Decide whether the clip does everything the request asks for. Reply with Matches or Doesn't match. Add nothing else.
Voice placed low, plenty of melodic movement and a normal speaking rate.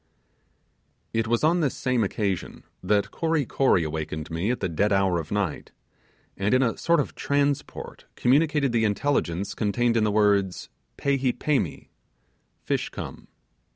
Matches